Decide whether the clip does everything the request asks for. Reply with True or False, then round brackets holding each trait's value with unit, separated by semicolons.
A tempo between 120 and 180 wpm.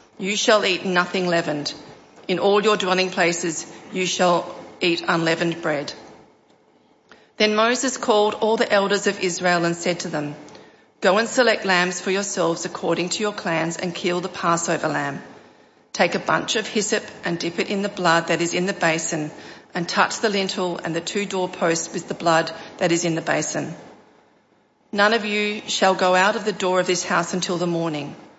False (190 wpm)